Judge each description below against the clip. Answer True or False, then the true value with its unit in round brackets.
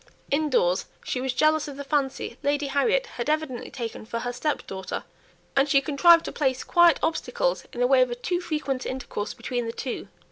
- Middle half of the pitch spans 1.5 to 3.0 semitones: False (3.8 semitones)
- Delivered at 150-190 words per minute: False (200 wpm)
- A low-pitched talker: False (275 Hz)